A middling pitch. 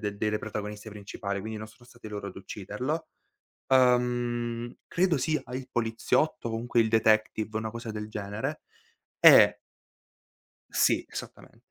No: low, 115 Hz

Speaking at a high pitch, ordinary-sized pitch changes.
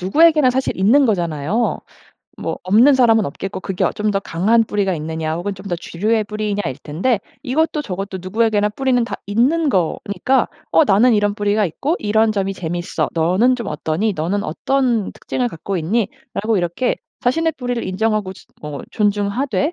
Yes: high, 205 Hz; average, 4.6 semitones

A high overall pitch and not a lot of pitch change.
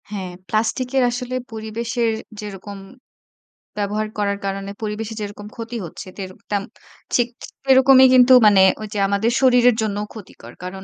No: high, 215 Hz; average, 3.2 semitones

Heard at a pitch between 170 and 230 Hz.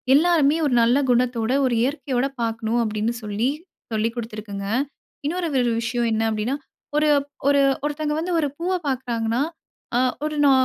No: high, 245 Hz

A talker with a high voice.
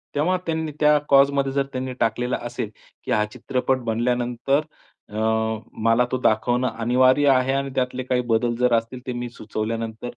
No: low, 125 Hz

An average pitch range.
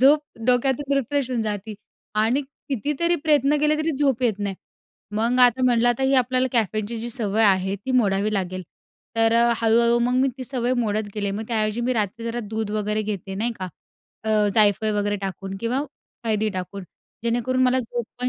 Yes: average, 3.4 semitones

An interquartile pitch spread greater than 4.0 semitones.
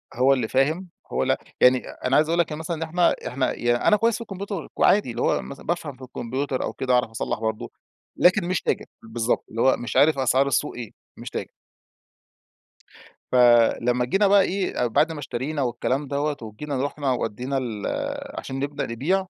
Yes: average, 4.8 semitones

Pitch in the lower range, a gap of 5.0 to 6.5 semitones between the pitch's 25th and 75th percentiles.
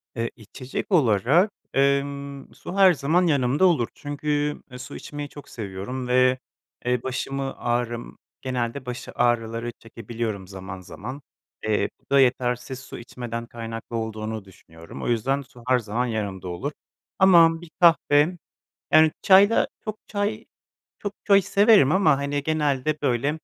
No: low, 130 Hz; average, 4.2 semitones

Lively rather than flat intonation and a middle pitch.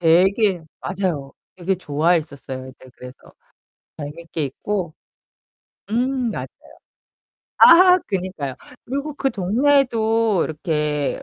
Yes: wide, 7.1 semitones; medium, 180 Hz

